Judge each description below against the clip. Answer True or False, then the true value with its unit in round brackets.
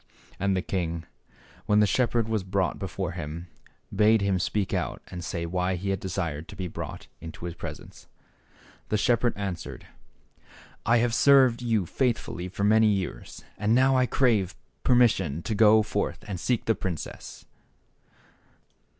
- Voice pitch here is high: False (100 Hz)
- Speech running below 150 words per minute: False (160 wpm)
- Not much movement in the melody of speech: False (3.9 semitones)